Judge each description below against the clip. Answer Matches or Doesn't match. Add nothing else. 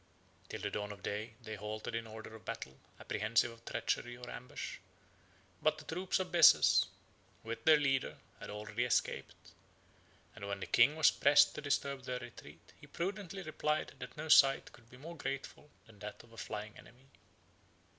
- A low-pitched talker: Matches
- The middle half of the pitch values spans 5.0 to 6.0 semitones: Matches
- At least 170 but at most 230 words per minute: Matches